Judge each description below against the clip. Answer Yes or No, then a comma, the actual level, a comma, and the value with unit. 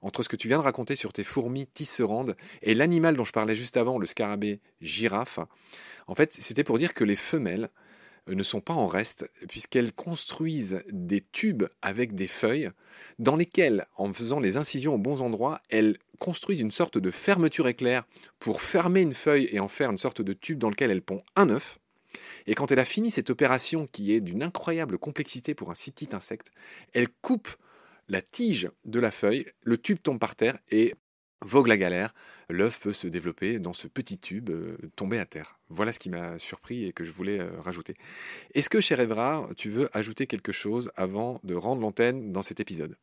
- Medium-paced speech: Yes, average, 200 wpm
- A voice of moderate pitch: No, low, 120 Hz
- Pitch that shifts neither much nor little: No, wide, 6.3 semitones